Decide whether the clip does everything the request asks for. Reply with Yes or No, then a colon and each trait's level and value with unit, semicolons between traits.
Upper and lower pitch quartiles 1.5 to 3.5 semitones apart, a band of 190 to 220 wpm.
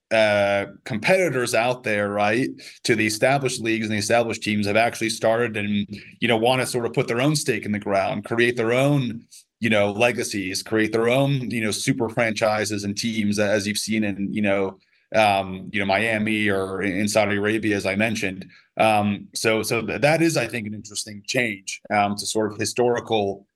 Yes: narrow, 2.4 semitones; average, 195 wpm